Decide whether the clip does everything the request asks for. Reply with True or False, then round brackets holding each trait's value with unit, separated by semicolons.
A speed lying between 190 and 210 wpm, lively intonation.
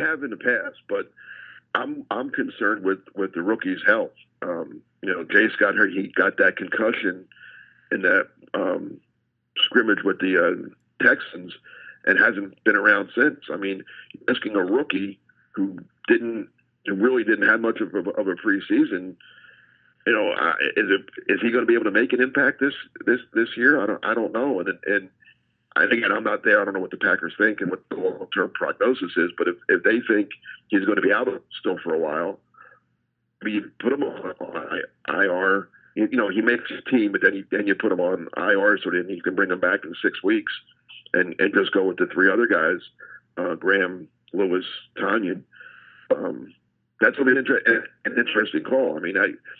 True (200 wpm; 7.1 semitones)